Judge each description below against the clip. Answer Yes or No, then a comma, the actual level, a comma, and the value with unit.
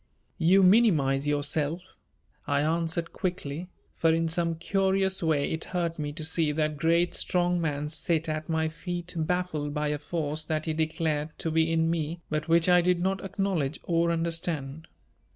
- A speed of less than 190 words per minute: Yes, average, 170 wpm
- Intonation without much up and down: Yes, narrow, 2.3 semitones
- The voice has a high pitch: No, medium, 165 Hz